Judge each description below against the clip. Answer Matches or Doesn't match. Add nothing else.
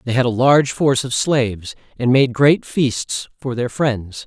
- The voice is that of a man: Matches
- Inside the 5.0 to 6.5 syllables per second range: Doesn't match